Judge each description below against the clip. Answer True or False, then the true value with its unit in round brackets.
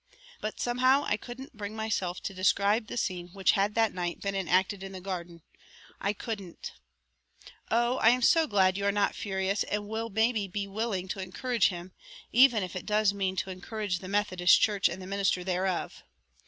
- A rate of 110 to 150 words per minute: False (190 wpm)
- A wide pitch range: False (2.9 semitones)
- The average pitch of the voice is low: False (200 Hz)